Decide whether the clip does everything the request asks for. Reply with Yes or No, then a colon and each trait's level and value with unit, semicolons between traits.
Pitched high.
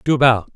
No: low, 125 Hz